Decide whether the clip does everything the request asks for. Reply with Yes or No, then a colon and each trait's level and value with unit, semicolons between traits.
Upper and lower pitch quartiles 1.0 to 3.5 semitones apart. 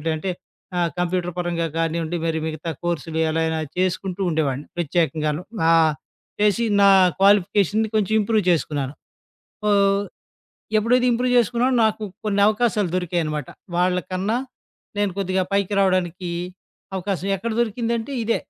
No: average, 4.0 semitones